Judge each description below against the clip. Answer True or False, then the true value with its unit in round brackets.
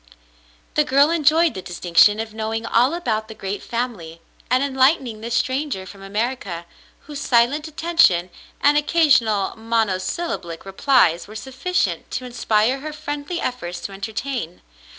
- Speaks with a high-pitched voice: True (235 Hz)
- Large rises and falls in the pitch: True (6.3 semitones)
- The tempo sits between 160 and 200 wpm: False (135 wpm)